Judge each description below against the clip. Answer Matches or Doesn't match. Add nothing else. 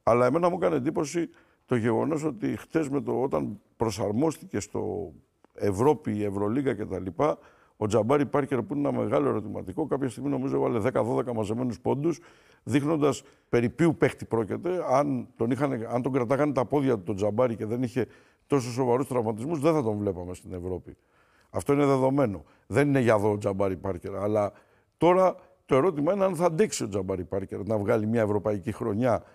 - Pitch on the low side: Matches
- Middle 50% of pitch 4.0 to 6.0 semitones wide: Matches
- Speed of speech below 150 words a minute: Doesn't match